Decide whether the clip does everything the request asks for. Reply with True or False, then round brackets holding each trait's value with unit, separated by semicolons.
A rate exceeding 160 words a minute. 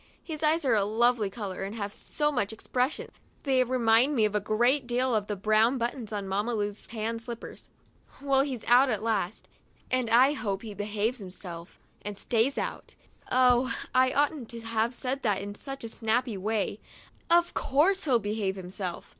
True (180 wpm)